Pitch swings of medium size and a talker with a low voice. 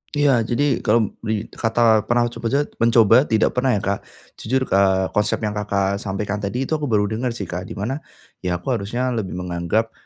Yes: average, 3.6 semitones; low, 110 Hz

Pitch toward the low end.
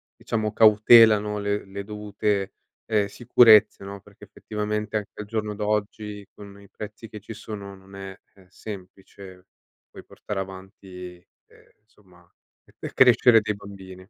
Yes: low, 105 Hz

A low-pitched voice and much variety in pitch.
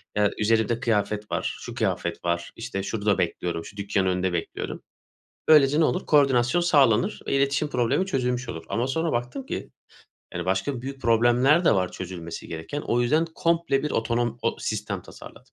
Yes: low, 120 Hz; wide, 5.7 semitones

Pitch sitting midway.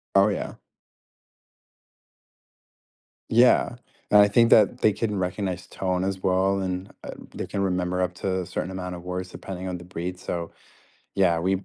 No: very low, 95 Hz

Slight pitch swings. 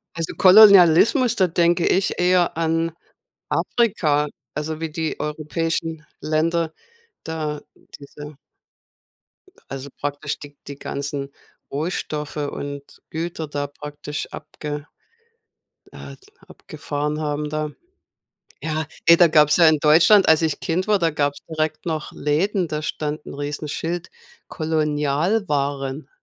Yes: narrow, 2.2 semitones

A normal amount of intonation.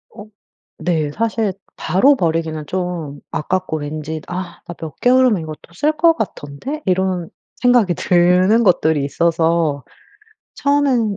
No: wide, 5.9 semitones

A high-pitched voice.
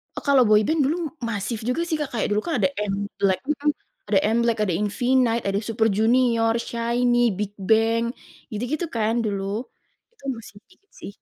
Yes: high, 230 Hz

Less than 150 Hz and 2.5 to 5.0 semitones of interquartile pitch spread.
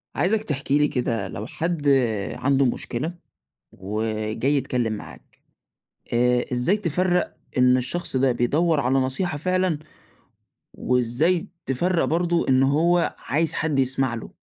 No: medium, 140 Hz; wide, 5.5 semitones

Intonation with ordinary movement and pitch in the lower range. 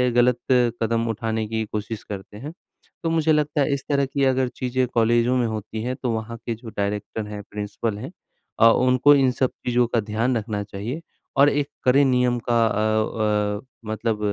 Yes: average, 3.0 semitones; low, 115 Hz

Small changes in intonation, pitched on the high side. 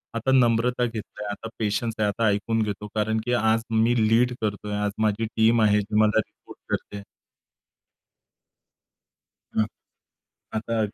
No: narrow, 1.7 semitones; low, 110 Hz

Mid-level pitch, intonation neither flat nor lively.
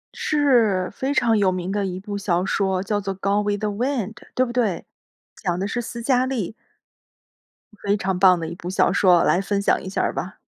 No: high, 200 Hz; average, 3.6 semitones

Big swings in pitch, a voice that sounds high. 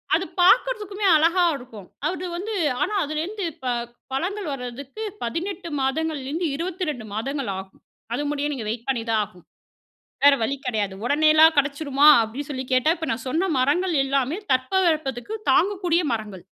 Yes: wide, 5.8 semitones; very high, 290 Hz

